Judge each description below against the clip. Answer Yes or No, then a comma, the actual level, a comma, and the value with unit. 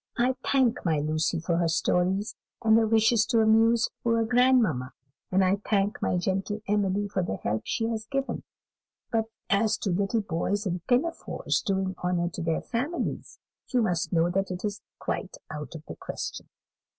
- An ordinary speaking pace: Yes, average, 170 wpm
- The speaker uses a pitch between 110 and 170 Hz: No, high, 200 Hz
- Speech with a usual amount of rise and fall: Yes, average, 4.2 semitones